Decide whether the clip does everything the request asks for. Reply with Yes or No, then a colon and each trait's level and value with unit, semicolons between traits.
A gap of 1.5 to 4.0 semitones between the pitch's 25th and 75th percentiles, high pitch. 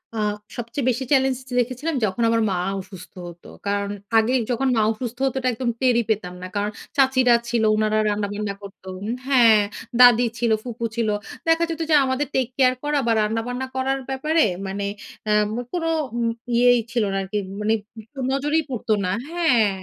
Yes: average, 3.7 semitones; high, 240 Hz